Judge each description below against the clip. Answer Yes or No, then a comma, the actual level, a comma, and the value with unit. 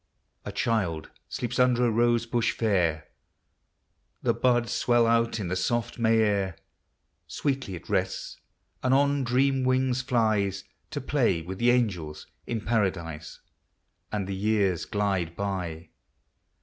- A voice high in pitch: No, low, 110 Hz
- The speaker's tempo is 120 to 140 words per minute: Yes, slow, 135 wpm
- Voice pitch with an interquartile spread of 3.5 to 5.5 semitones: Yes, average, 4.3 semitones